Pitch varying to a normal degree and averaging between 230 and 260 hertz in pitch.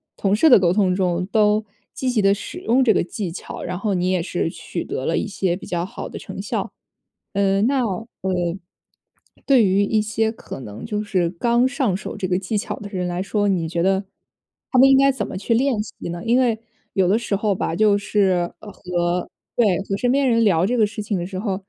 No: average, 3.5 semitones; high, 200 Hz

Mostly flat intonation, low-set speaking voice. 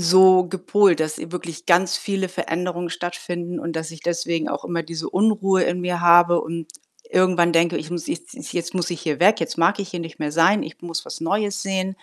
No: narrow, 2.0 semitones; medium, 175 Hz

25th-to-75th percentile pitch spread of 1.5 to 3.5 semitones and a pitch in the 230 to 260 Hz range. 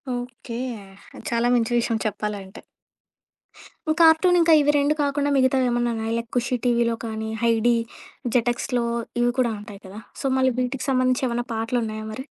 Yes: narrow, 2.4 semitones; high, 240 Hz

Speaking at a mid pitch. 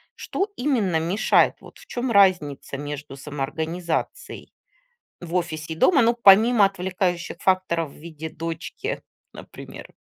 Yes: medium, 175 Hz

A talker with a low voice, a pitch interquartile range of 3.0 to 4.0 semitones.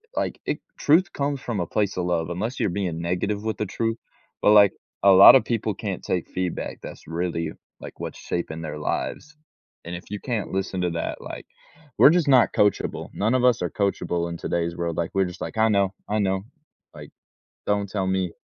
Yes: very low, 95 Hz; average, 3.7 semitones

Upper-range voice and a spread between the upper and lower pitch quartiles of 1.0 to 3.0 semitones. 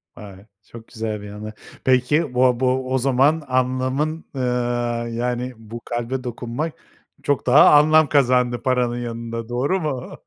No: low, 125 Hz; narrow, 2.4 semitones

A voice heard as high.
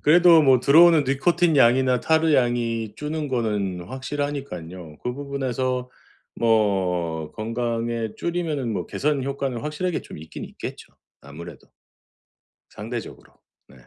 No: low, 125 Hz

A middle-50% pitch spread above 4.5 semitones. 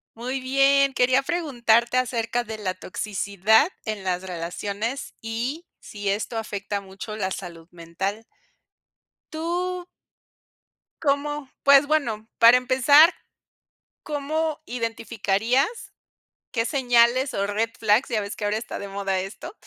Yes: average, 5.2 semitones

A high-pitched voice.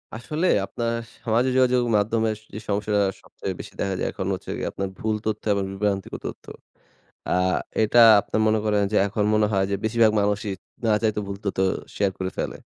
No: low, 105 Hz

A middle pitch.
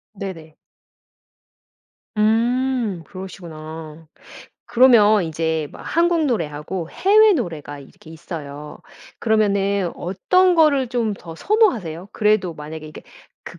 No: high, 195 Hz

